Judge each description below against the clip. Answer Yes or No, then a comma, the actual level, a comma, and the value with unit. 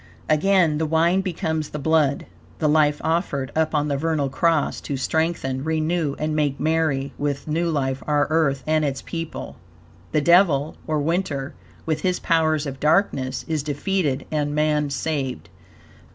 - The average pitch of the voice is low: No, medium, 155 Hz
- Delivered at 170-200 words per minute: No, average, 155 wpm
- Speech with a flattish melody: Yes, narrow, 2.3 semitones